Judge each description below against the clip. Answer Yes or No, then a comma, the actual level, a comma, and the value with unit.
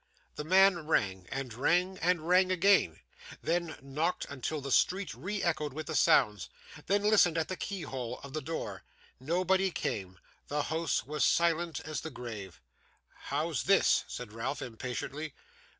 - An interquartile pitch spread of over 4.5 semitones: Yes, wide, 5.6 semitones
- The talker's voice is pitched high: No, medium, 155 Hz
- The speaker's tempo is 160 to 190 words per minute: No, average, 150 wpm